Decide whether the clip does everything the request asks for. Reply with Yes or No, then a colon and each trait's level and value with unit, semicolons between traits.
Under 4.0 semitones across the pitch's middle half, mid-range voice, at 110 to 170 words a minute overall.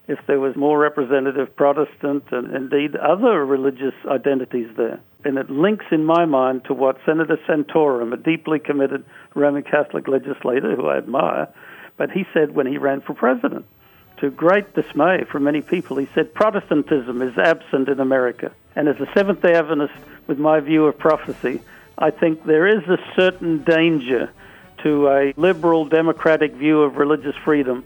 Yes: average, 2.7 semitones; medium, 145 Hz; average, 165 wpm